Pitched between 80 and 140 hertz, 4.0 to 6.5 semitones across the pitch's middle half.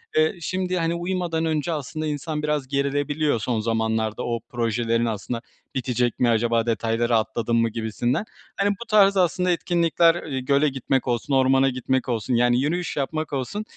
Yes: low, 135 Hz; average, 5.3 semitones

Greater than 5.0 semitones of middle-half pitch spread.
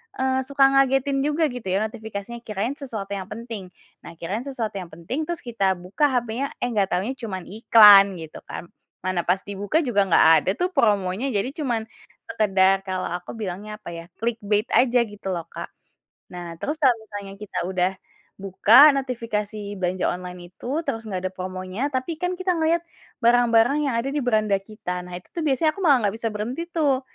Yes: wide, 5.6 semitones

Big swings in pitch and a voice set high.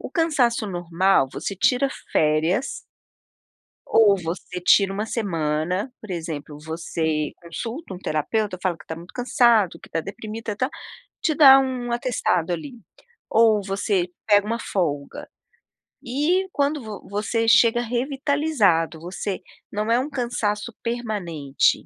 Yes: wide, 5.8 semitones; high, 210 Hz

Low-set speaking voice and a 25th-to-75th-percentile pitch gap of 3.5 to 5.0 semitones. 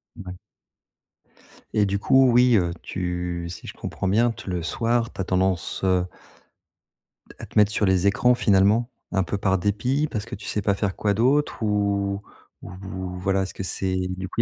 No: low, 100 Hz; average, 2.9 semitones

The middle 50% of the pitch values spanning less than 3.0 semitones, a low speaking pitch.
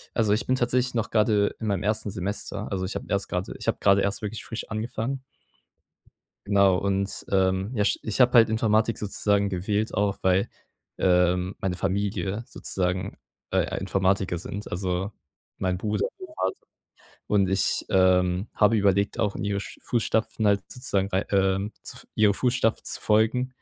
Yes: narrow, 2.5 semitones; low, 100 Hz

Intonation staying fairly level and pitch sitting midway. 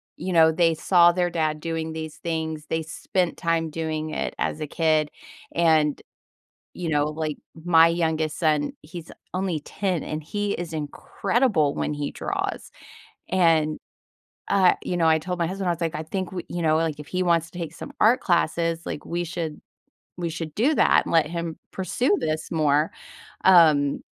Yes: narrow, 2.0 semitones; medium, 165 Hz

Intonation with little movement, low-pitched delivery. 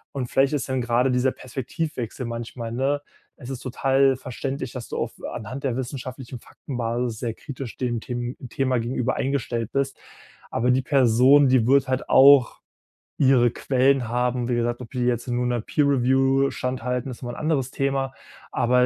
Yes: narrow, 1.9 semitones; low, 125 Hz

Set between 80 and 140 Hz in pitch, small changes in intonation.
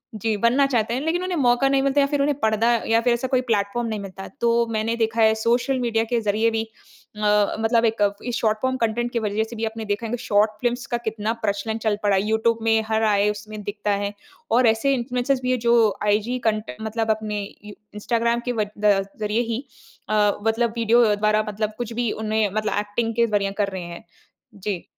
No: high, 225 Hz; narrow, 2.2 semitones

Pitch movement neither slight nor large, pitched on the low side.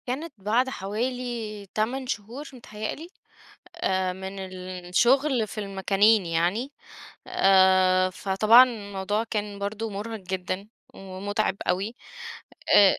No: average, 3.3 semitones; high, 205 Hz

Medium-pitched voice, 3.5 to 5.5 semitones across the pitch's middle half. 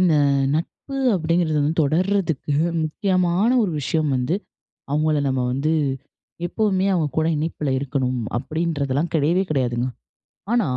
Yes: medium, 155 Hz; average, 3.8 semitones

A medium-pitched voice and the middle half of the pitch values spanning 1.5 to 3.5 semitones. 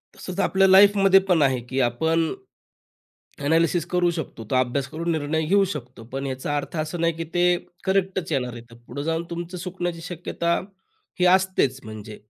No: medium, 165 Hz; average, 4.9 semitones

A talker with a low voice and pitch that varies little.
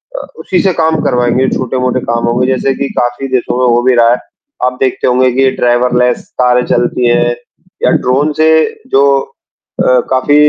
Yes: low, 125 Hz; narrow, 1.4 semitones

